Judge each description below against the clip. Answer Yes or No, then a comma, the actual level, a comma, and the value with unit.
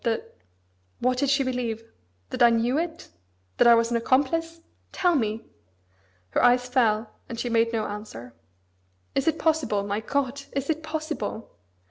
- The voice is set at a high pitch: Yes, high, 245 Hz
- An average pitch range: Yes, average, 3.8 semitones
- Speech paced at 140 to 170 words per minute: Yes, average, 160 wpm